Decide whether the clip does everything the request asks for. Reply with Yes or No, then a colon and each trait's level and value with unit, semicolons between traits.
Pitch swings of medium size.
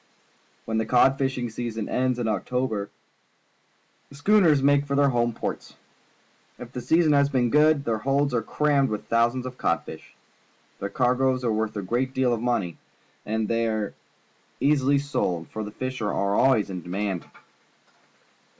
Yes: average, 3.9 semitones